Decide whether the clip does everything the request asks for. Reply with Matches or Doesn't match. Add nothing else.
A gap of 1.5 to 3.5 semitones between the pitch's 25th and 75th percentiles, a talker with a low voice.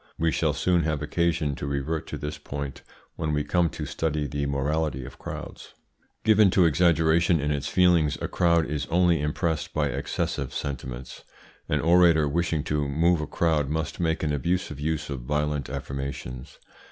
Matches